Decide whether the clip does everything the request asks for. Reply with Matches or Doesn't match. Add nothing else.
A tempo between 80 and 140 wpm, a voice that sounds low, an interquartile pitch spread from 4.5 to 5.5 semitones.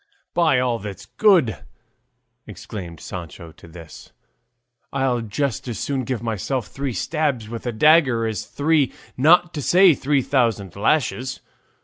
Matches